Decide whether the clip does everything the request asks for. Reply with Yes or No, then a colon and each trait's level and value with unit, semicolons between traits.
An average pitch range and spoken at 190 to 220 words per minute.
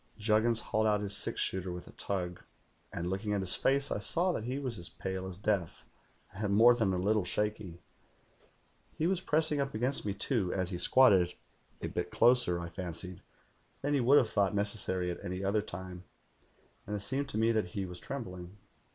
Yes: average, 4.5 semitones; average, 200 wpm